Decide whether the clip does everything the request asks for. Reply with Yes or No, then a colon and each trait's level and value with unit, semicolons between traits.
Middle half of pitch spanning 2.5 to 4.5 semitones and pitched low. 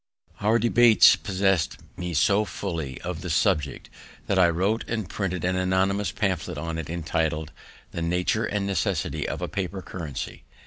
Yes: average, 3.1 semitones; very low, 90 Hz